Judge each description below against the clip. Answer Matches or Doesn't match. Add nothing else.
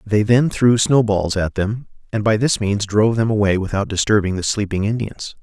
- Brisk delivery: Matches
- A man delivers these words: Matches